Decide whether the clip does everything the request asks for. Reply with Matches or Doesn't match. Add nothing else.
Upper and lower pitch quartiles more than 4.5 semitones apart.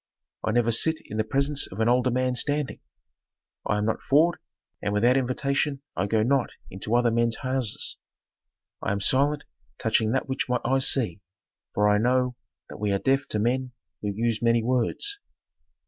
Doesn't match